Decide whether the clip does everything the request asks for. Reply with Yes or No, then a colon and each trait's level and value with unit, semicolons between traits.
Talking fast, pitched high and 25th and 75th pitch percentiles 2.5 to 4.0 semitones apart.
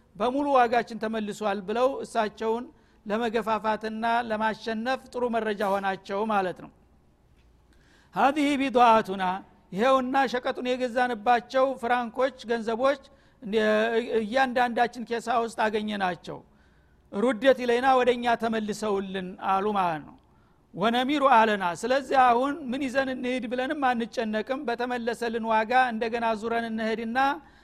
No: average, 100 wpm; high, 230 Hz; average, 2.8 semitones